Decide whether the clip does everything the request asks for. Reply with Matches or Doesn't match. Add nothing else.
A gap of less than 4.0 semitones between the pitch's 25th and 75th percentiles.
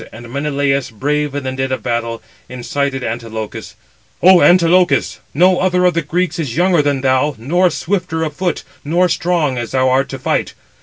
Doesn't match